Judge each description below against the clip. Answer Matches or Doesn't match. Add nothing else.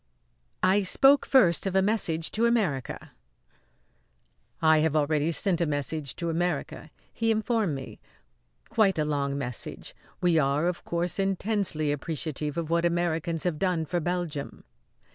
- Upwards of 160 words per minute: Doesn't match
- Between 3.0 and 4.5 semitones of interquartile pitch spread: Matches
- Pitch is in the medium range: Matches